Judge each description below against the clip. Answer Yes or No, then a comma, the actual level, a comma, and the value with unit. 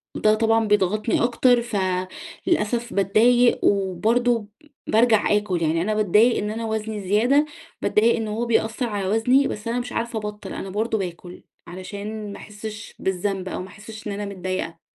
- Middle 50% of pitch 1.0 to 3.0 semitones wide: Yes, average, 2.7 semitones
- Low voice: No, high, 215 Hz